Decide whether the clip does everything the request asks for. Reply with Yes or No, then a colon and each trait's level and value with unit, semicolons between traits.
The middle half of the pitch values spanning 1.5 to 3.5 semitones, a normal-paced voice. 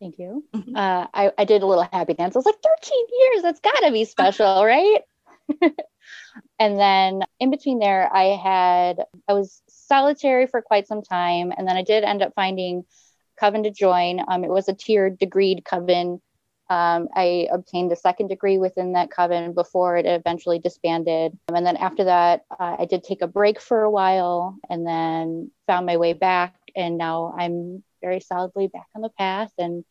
Yes: average, 2.9 semitones; average, 190 wpm